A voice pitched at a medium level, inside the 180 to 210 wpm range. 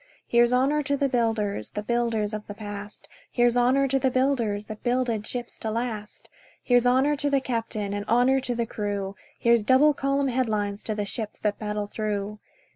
No: high, 235 Hz; average, 195 wpm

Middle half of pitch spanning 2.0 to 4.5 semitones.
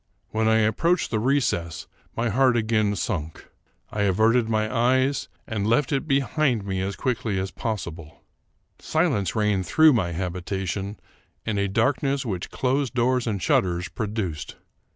No: average, 4.9 semitones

